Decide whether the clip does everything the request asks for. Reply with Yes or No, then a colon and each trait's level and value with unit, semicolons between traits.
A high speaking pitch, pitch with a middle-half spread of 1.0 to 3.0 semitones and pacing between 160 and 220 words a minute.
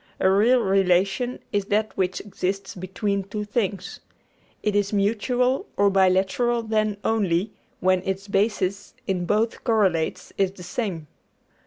No: high, 200 Hz; narrow, 2.4 semitones; slow, 135 wpm